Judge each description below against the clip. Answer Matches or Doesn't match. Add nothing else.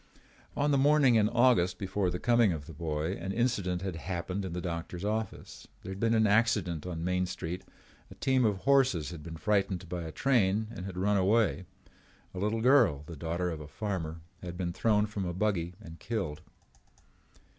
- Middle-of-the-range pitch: Doesn't match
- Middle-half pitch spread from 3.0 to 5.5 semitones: Matches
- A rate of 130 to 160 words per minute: Doesn't match